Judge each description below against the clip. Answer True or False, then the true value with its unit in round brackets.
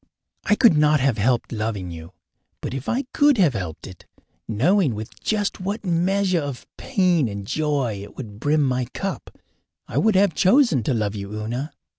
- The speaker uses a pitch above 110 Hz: True (140 Hz)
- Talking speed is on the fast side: False (180 wpm)